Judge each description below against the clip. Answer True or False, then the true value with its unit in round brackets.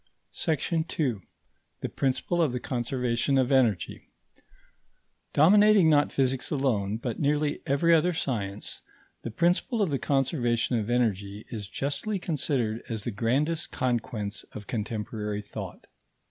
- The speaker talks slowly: True (130 wpm)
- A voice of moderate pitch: False (130 Hz)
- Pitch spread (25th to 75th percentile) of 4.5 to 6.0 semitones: True (5.2 semitones)